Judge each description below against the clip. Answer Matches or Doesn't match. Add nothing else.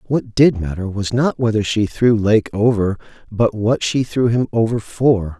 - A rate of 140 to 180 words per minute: Doesn't match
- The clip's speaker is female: Doesn't match